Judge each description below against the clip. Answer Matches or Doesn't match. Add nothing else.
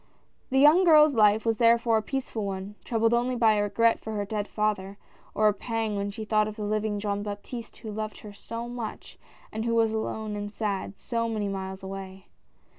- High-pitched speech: Matches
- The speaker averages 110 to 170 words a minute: Doesn't match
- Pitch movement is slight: Matches